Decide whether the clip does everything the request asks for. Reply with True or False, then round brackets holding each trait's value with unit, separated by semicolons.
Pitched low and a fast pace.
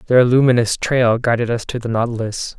False (120 Hz; 185 wpm)